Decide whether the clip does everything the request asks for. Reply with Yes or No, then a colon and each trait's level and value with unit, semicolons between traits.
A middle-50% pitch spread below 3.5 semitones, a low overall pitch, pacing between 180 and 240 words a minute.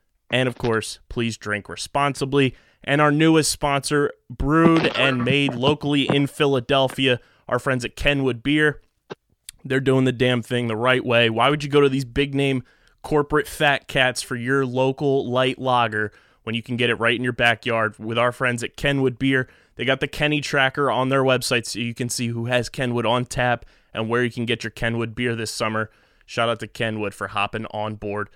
Yes: average, 3.1 semitones; low, 125 Hz; average, 200 wpm